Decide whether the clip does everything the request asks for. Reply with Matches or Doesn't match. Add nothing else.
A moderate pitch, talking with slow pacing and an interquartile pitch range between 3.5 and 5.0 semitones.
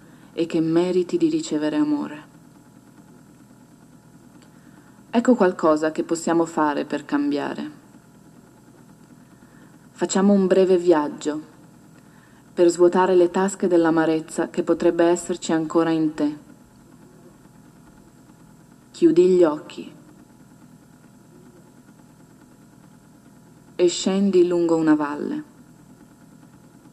Doesn't match